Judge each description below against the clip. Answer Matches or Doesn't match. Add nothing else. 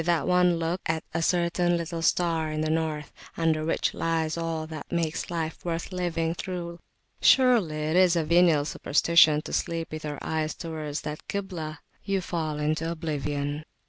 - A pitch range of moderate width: Doesn't match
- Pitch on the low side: Doesn't match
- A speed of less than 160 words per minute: Doesn't match